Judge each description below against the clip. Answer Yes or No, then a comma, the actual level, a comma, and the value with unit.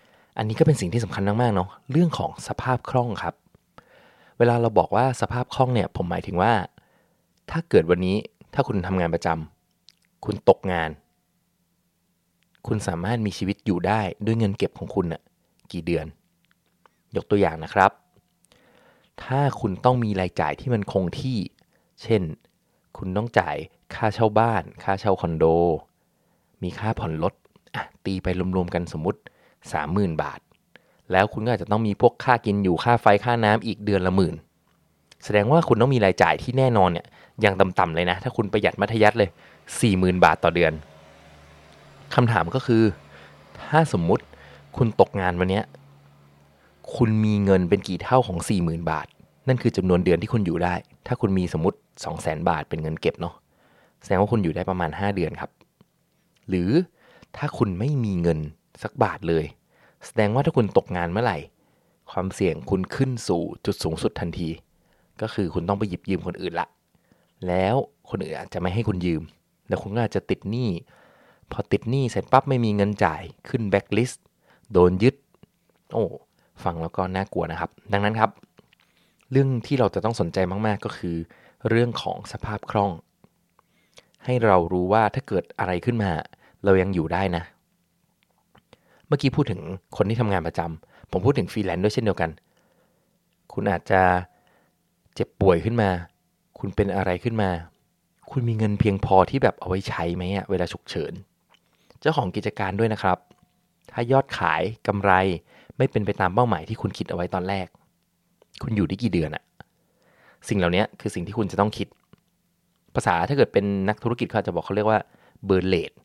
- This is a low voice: Yes, low, 100 Hz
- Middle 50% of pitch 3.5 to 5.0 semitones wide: Yes, average, 4.2 semitones